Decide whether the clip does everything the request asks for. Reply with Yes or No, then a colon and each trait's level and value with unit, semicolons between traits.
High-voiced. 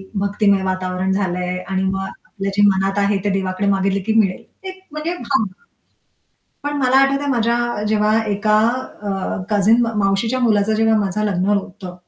Yes: high, 205 Hz